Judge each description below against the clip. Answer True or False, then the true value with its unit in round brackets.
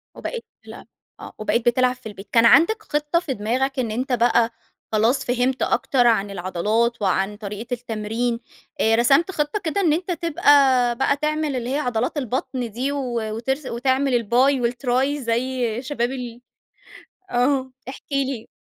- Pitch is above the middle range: True (245 Hz)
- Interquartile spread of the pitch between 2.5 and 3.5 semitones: True (3.2 semitones)